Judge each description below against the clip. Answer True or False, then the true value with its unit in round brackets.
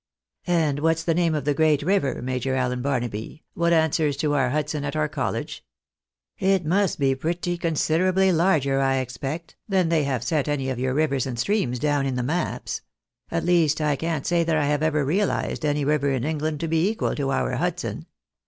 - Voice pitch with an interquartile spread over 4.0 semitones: False (3.5 semitones)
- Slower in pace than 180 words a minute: False (200 wpm)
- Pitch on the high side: False (150 Hz)